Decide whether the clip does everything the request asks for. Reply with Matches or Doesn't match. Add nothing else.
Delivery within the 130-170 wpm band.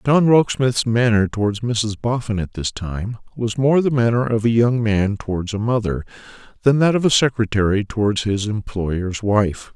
Doesn't match